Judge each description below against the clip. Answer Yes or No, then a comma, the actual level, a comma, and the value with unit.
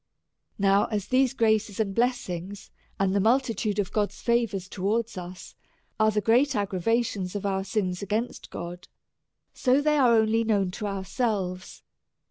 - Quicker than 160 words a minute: No, average, 155 wpm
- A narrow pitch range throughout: No, average, 3.3 semitones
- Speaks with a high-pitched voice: Yes, high, 210 Hz